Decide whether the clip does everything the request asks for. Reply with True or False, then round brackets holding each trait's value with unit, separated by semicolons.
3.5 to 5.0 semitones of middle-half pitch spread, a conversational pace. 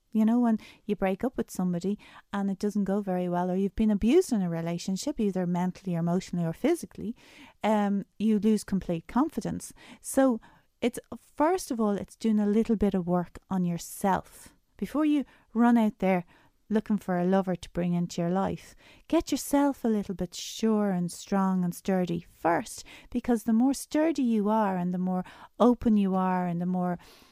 True (4.1 semitones; 190 wpm)